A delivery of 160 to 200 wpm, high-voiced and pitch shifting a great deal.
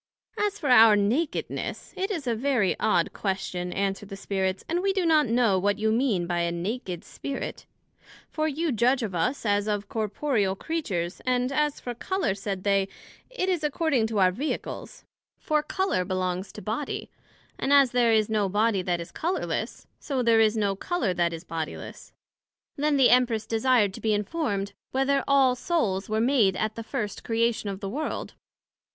Yes: average, 180 wpm; high, 225 Hz; wide, 6.0 semitones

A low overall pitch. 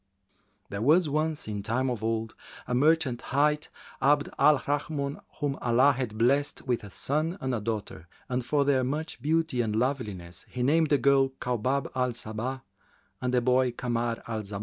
Yes: low, 130 Hz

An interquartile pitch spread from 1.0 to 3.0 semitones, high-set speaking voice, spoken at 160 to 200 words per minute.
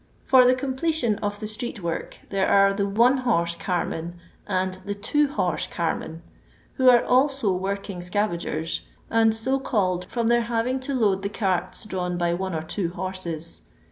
No: average, 4.9 semitones; high, 200 Hz; average, 170 wpm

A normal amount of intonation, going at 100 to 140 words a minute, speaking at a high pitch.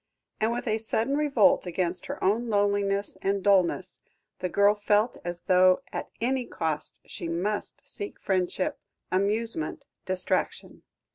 Yes: average, 3.1 semitones; slow, 135 wpm; high, 200 Hz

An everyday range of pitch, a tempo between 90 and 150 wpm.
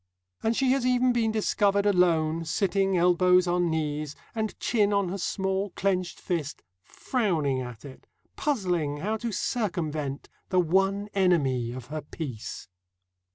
Yes: average, 4.7 semitones; average, 140 wpm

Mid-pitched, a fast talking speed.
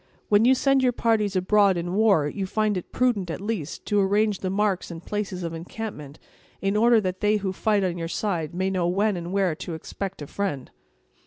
No: high, 195 Hz; fast, 215 wpm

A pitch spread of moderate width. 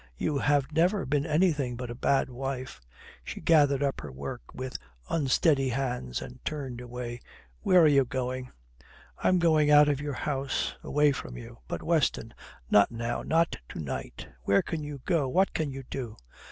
Yes: average, 3.2 semitones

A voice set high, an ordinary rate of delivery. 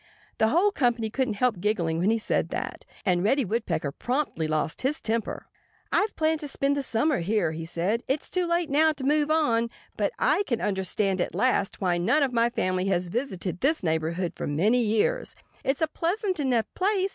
Yes: high, 230 Hz; average, 195 wpm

